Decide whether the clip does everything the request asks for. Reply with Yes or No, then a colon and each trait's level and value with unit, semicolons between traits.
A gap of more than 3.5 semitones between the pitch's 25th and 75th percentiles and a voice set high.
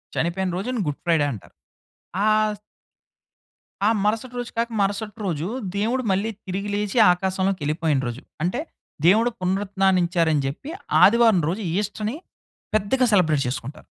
Yes: average, 4.0 semitones; high, 195 Hz